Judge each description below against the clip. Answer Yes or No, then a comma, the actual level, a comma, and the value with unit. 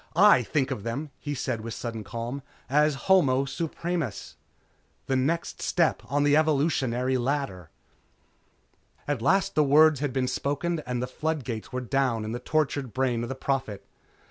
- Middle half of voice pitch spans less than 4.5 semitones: Yes, average, 3.6 semitones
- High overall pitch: No, low, 135 Hz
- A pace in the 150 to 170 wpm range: Yes, average, 165 wpm